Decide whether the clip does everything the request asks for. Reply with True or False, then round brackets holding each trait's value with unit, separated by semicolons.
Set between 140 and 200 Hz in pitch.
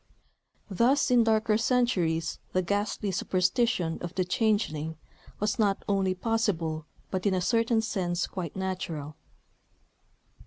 True (190 Hz)